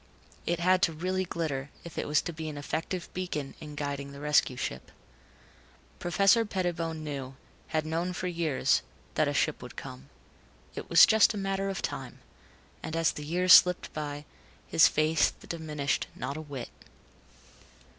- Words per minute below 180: Yes, average, 165 wpm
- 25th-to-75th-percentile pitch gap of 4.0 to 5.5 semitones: No, average, 3.6 semitones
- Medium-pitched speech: Yes, medium, 160 Hz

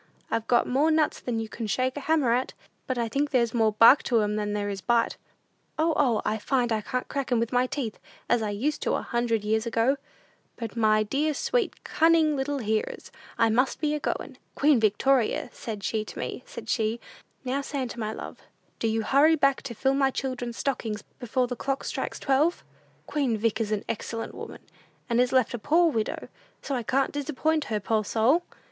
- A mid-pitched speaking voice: No, high, 245 Hz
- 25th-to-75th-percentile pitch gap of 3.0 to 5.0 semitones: Yes, average, 3.8 semitones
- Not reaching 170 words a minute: No, fast, 205 wpm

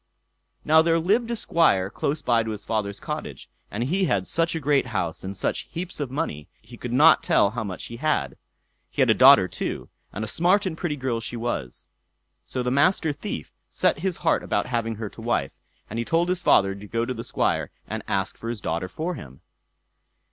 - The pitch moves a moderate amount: No, wide, 7.8 semitones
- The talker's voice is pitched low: Yes, low, 120 Hz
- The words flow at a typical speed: No, fast, 215 wpm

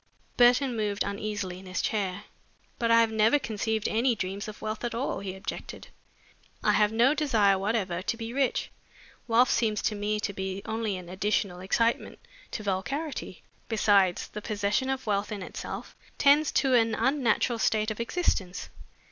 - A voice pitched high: Yes, high, 215 Hz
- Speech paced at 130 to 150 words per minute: No, average, 165 wpm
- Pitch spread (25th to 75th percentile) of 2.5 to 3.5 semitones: Yes, average, 2.8 semitones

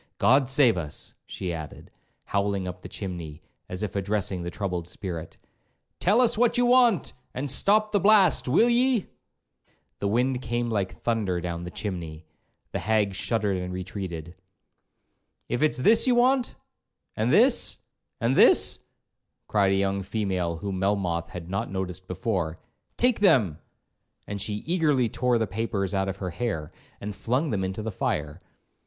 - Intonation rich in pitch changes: Yes, wide, 5.9 semitones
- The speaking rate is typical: Yes, average, 155 wpm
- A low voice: Yes, low, 100 Hz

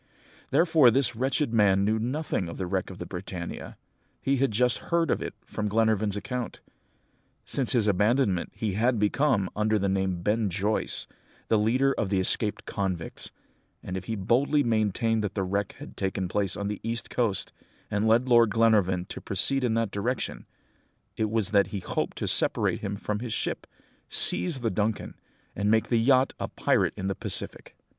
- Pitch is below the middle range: Yes, low, 110 Hz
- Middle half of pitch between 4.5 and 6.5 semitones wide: No, average, 3.3 semitones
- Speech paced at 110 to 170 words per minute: No, average, 185 wpm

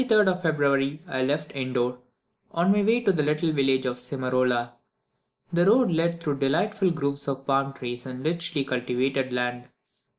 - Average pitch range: Yes, average, 4.7 semitones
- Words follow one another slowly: No, average, 175 wpm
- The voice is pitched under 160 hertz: Yes, medium, 140 Hz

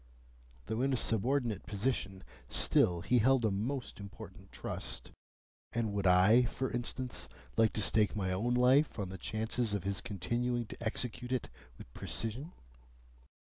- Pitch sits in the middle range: No, low, 115 Hz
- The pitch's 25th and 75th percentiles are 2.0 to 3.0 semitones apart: No, average, 3.7 semitones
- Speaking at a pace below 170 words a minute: Yes, average, 150 wpm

